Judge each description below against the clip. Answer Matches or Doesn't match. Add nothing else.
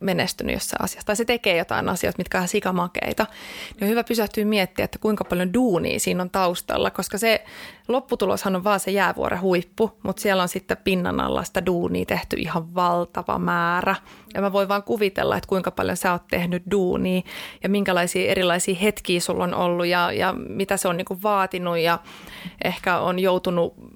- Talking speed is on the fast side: Matches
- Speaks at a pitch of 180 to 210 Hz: Matches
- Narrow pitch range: Matches